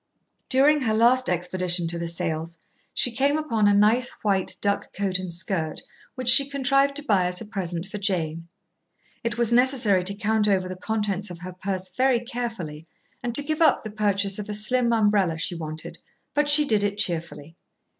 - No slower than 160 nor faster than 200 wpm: Yes, average, 190 wpm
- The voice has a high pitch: Yes, high, 205 Hz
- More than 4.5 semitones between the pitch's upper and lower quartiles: Yes, average, 5.1 semitones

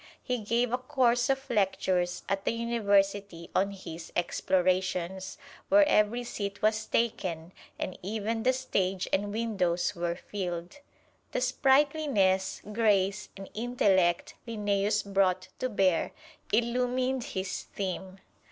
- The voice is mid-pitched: No, high, 200 Hz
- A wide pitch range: No, average, 4.0 semitones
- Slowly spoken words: Yes, slow, 120 wpm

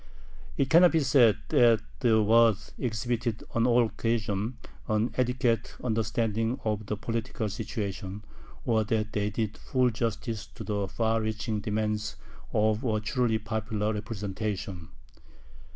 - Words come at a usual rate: No, slow, 130 wpm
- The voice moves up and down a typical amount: No, narrow, 1.8 semitones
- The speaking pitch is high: No, low, 110 Hz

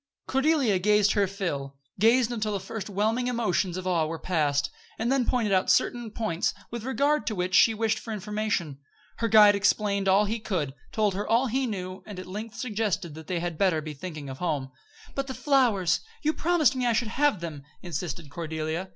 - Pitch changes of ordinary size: Yes, average, 4.7 semitones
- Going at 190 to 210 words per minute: Yes, average, 200 wpm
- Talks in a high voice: Yes, high, 205 Hz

